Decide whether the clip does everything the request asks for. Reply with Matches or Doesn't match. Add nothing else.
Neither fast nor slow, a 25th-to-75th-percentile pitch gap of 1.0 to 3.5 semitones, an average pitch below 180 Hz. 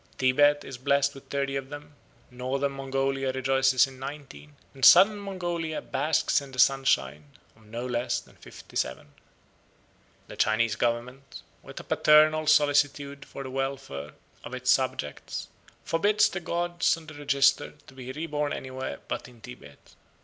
Matches